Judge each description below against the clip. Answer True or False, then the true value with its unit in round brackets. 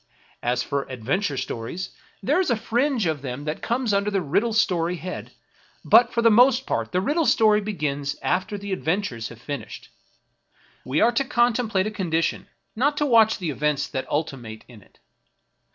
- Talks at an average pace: True (175 wpm)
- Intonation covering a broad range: True (8.2 semitones)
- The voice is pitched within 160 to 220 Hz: True (190 Hz)